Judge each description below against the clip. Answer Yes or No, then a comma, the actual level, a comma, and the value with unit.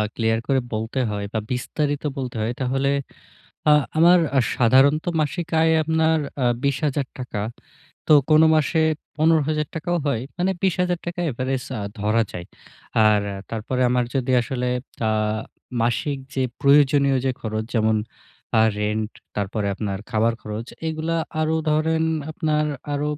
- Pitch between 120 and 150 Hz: Yes, low, 135 Hz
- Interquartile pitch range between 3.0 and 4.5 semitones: No, wide, 5.5 semitones